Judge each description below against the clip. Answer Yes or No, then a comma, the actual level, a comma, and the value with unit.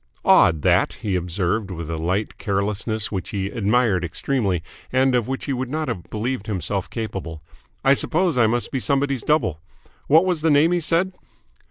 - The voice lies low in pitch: Yes, low, 110 Hz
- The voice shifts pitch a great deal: Yes, wide, 6.4 semitones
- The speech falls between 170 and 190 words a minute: Yes, average, 180 wpm